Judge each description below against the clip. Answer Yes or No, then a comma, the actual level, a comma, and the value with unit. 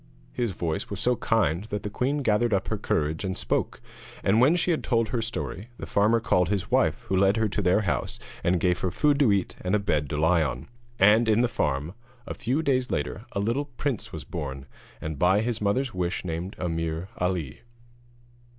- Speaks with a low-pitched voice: Yes, low, 100 Hz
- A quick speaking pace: Yes, fast, 210 wpm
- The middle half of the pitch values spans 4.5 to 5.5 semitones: Yes, average, 5.1 semitones